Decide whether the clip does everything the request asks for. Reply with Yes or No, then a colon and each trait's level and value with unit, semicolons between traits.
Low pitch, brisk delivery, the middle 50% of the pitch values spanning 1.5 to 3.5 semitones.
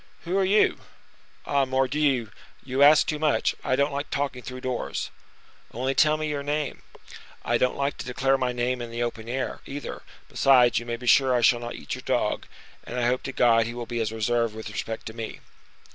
Yes: low, 125 Hz; fast, 215 wpm; average, 3.0 semitones